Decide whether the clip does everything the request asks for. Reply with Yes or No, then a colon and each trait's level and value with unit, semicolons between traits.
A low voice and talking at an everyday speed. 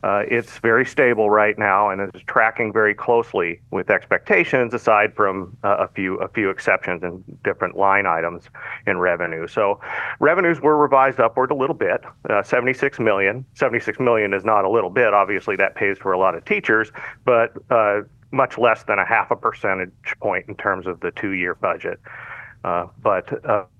Yes: low, 105 Hz; average, 180 wpm